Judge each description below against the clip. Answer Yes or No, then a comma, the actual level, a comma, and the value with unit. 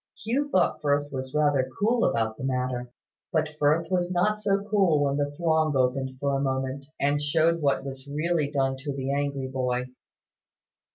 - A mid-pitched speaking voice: Yes, medium, 145 Hz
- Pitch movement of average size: Yes, average, 3.8 semitones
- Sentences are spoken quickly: No, average, 175 wpm